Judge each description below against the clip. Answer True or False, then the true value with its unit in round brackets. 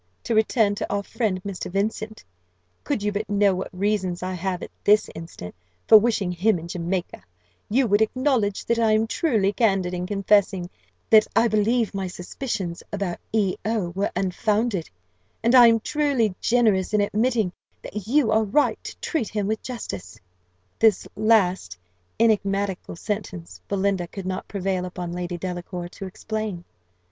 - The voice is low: False (200 Hz)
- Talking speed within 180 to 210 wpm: False (160 wpm)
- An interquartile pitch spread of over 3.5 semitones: False (3.1 semitones)